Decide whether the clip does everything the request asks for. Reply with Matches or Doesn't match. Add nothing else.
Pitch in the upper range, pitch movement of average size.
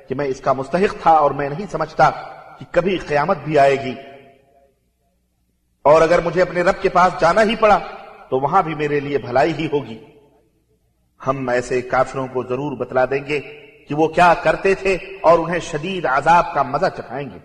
Doesn't match